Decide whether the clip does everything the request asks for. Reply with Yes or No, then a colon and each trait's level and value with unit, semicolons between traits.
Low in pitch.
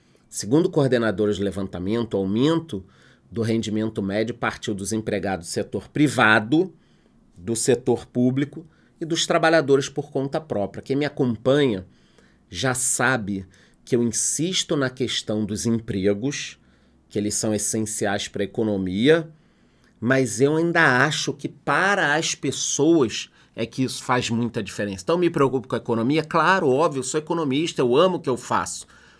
Yes: low, 125 Hz